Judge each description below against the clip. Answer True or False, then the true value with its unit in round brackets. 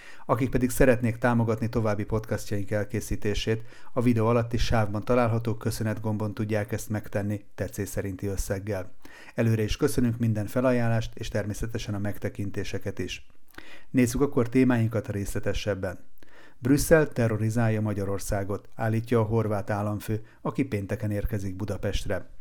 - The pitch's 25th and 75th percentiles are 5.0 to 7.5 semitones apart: False (2.5 semitones)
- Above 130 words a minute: False (120 wpm)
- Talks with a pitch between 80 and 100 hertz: False (110 Hz)